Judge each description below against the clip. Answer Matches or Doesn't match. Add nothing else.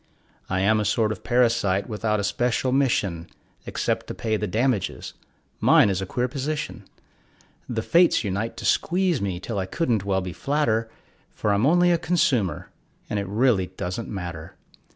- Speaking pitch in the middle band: Doesn't match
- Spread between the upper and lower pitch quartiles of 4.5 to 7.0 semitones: Matches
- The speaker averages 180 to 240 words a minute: Doesn't match